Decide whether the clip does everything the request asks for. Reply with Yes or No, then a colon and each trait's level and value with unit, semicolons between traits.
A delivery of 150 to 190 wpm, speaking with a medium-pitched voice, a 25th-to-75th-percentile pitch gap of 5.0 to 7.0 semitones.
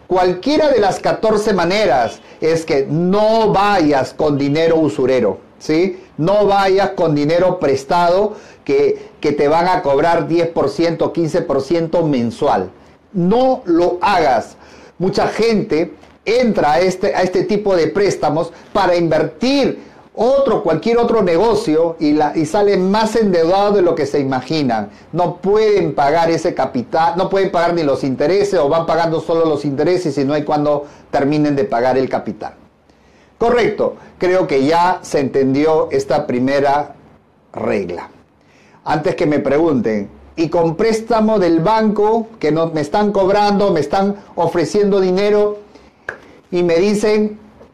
No: average, 140 wpm; medium, 175 Hz; average, 5.3 semitones